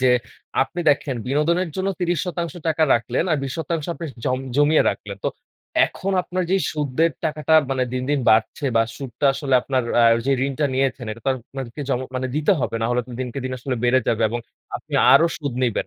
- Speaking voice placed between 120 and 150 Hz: Yes, medium, 140 Hz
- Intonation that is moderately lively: Yes, average, 4.1 semitones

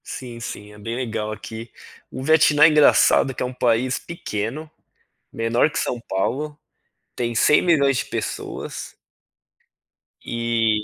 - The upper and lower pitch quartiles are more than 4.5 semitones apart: No, average, 3.7 semitones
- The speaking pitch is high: No, low, 120 Hz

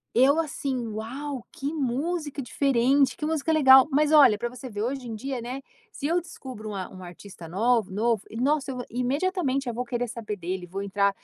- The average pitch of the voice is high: Yes, very high, 250 Hz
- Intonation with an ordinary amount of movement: Yes, average, 4.4 semitones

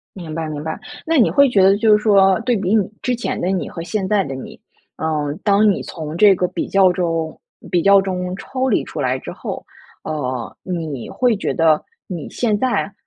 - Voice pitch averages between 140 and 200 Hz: Yes, medium, 185 Hz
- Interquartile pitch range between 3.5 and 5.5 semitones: Yes, average, 4.8 semitones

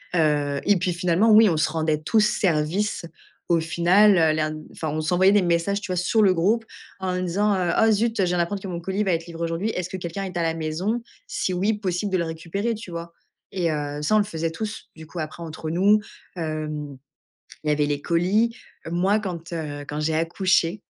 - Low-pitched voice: No, medium, 175 Hz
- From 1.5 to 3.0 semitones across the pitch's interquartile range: No, average, 3.7 semitones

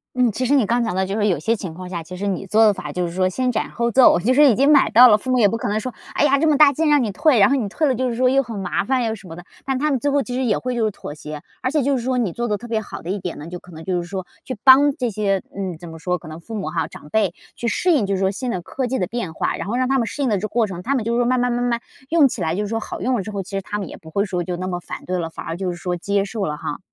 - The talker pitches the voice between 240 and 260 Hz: No, high, 215 Hz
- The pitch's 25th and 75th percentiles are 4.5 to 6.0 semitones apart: Yes, wide, 5.5 semitones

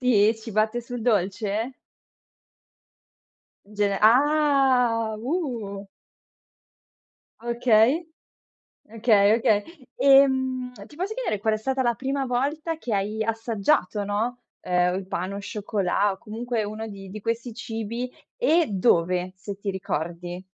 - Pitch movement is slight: No, average, 4.0 semitones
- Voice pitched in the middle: No, high, 225 Hz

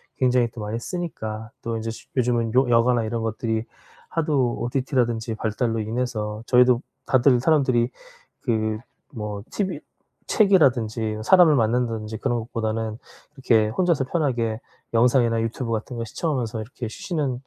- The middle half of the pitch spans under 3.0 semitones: Yes, narrow, 2.6 semitones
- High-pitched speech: No, low, 120 Hz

